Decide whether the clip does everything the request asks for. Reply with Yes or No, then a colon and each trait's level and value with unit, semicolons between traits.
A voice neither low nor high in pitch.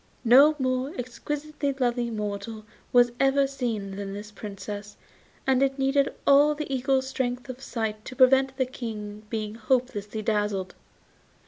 No: high, 245 Hz